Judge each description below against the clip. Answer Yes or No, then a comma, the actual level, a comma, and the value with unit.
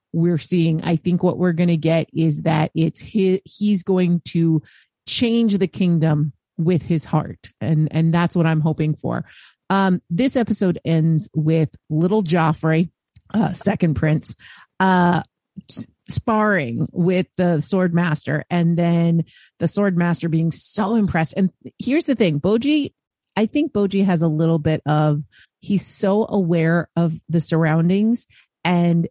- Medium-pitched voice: Yes, medium, 170 Hz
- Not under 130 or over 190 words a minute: Yes, average, 150 wpm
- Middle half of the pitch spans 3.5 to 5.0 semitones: No, average, 3.1 semitones